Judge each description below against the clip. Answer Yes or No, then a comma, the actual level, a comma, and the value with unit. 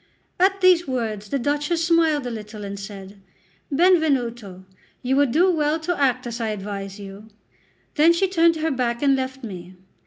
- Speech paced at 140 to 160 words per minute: No, average, 175 wpm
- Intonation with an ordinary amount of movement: No, wide, 7.3 semitones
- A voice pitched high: Yes, very high, 260 Hz